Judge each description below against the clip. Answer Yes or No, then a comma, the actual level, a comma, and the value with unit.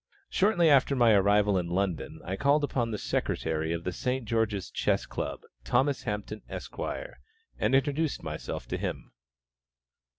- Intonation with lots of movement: Yes, wide, 6.2 semitones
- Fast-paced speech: No, average, 145 wpm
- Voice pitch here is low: Yes, low, 110 Hz